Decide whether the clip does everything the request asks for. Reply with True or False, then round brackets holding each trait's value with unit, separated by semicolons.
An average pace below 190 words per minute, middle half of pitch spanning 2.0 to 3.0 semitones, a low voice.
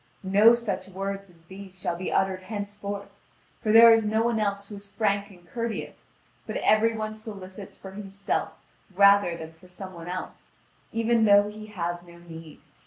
False (175 wpm; 2.6 semitones; 200 Hz)